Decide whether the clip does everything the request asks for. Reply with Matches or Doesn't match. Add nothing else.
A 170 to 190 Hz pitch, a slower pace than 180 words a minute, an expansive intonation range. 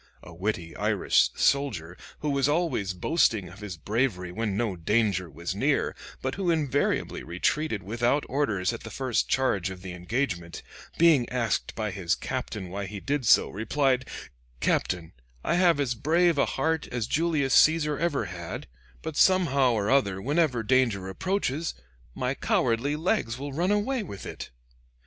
Doesn't match